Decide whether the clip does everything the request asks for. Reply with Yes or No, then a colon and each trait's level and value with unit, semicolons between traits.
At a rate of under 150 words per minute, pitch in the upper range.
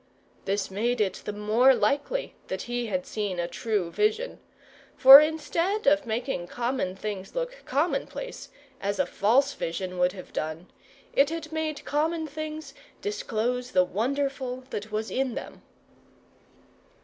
Yes: average, 140 wpm; very high, 250 Hz